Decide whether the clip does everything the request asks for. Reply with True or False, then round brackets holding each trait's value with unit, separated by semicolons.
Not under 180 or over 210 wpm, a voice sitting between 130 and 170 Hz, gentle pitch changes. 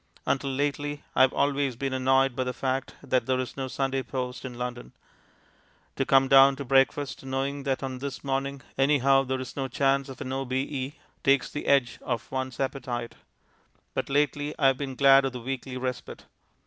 True (185 wpm; 135 Hz; 1.1 semitones)